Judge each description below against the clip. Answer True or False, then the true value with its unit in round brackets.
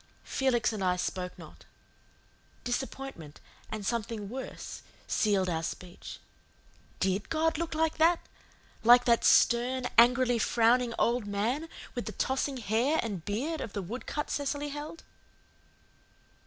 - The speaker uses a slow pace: True (130 wpm)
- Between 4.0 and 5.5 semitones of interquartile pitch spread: True (4.8 semitones)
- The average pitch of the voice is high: True (240 Hz)